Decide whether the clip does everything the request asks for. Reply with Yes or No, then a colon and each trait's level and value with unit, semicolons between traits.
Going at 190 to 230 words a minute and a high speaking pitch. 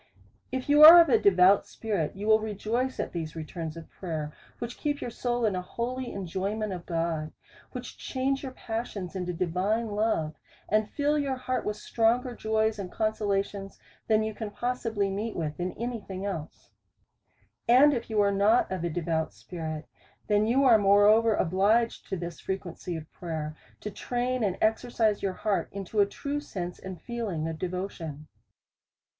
No: average, 175 wpm; high, 205 Hz